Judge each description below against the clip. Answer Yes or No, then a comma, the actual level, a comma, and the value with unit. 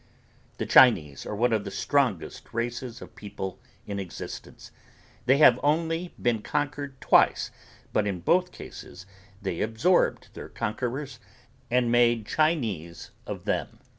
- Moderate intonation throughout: No, wide, 5.7 semitones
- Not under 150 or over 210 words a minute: No, slow, 135 wpm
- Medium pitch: No, low, 120 Hz